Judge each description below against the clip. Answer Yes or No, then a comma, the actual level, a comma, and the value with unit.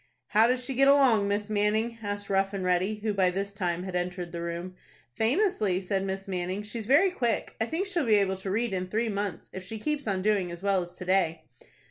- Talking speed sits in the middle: No, fast, 230 wpm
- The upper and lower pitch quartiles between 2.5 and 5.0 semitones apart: Yes, average, 3.2 semitones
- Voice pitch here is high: Yes, high, 200 Hz